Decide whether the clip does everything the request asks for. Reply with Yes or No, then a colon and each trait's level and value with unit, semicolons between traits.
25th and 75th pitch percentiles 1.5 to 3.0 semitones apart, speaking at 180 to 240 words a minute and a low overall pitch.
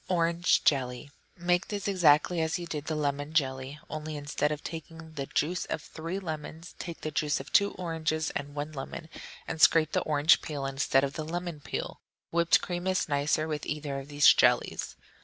No: average, 2.7 semitones; average, 190 wpm; medium, 155 Hz